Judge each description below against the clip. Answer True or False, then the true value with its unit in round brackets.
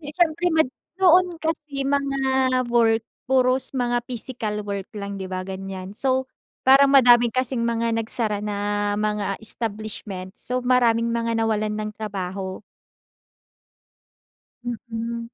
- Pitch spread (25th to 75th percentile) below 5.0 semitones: True (3.7 semitones)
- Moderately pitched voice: False (230 Hz)